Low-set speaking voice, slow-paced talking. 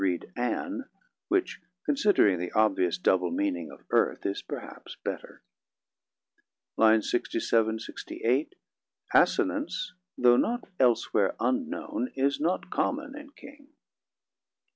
Yes: low, 125 Hz; slow, 105 wpm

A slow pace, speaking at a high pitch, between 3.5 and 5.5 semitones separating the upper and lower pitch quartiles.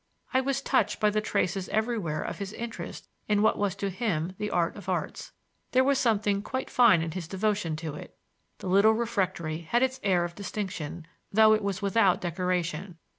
No: average, 190 wpm; high, 200 Hz; average, 3.8 semitones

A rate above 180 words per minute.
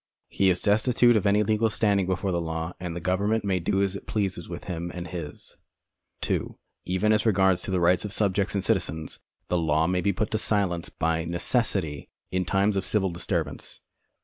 Yes: average, 195 wpm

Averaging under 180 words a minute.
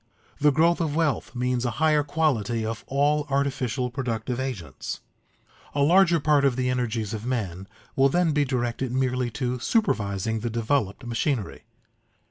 Yes: average, 150 wpm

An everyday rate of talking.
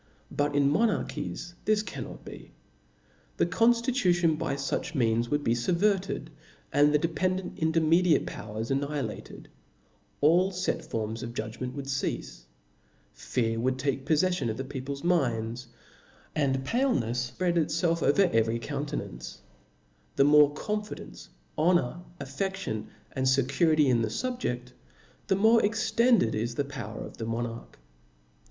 No: slow, 130 wpm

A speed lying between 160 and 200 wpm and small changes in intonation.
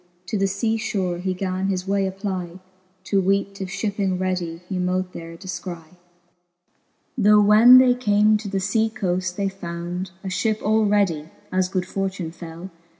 Yes: average, 165 wpm; narrow, 2.2 semitones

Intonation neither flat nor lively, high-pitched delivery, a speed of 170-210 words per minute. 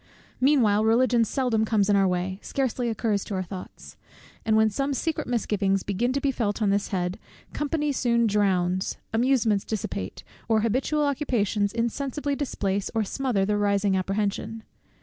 No: average, 4.1 semitones; high, 220 Hz; average, 155 wpm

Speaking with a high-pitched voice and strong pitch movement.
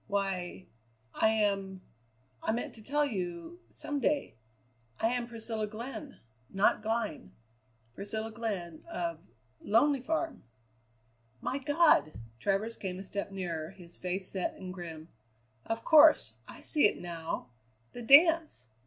Yes: high, 215 Hz; wide, 6.2 semitones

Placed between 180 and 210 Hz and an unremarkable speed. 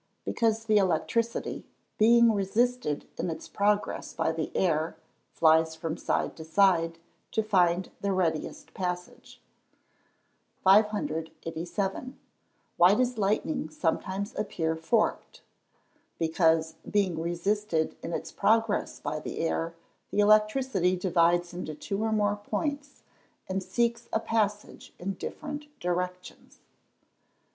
No: high, 190 Hz; slow, 115 wpm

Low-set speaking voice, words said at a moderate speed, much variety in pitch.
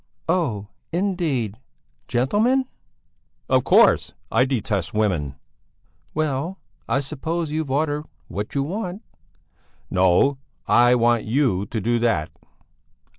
No: low, 130 Hz; slow, 105 wpm; wide, 6.5 semitones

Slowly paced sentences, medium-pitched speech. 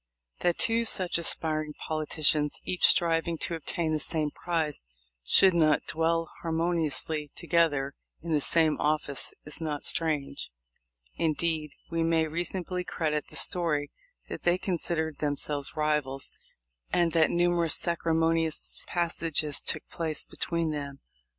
Yes: slow, 130 wpm; medium, 160 Hz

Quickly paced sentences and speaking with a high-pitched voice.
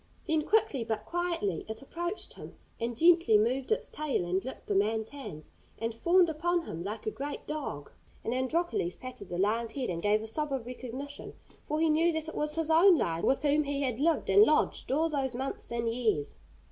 Yes: fast, 210 wpm; very high, 270 Hz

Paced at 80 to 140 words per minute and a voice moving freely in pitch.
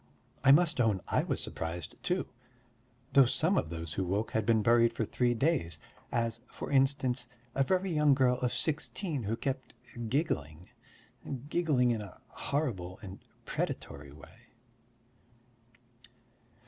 Yes: slow, 135 wpm; wide, 6.4 semitones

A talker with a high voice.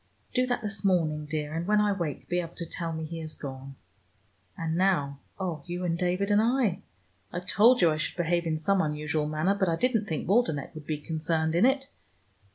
No: medium, 170 Hz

